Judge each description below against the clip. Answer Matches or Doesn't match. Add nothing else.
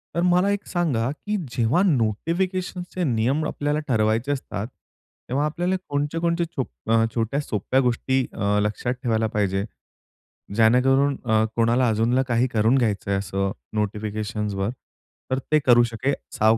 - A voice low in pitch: Matches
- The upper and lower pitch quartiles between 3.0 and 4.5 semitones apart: Doesn't match